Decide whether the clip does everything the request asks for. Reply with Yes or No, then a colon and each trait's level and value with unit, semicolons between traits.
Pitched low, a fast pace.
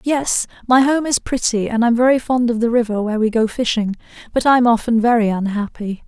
No: high, 235 Hz; fast, 210 wpm